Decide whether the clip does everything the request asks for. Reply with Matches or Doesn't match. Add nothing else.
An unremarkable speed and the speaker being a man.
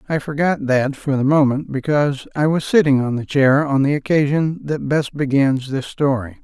Matches